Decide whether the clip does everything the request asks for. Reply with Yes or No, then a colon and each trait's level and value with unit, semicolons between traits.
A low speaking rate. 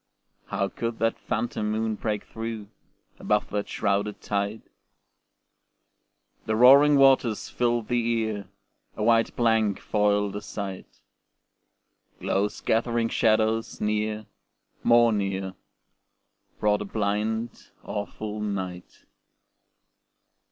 Yes: slow, 100 wpm